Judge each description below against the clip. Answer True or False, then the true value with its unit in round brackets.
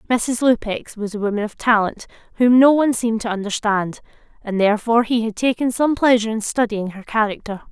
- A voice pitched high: True (225 Hz)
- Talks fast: False (185 wpm)